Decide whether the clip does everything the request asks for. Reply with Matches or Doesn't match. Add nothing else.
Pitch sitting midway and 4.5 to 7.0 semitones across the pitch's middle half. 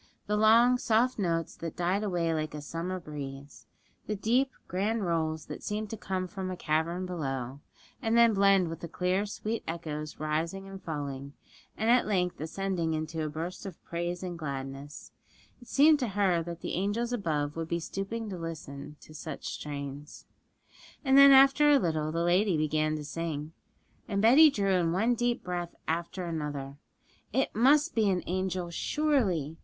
Matches